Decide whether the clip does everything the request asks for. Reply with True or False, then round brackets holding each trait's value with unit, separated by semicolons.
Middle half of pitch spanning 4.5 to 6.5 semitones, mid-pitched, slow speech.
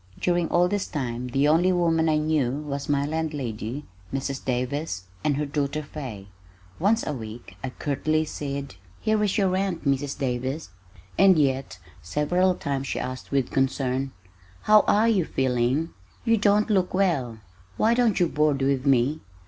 False (4.8 semitones; 145 Hz; 160 wpm)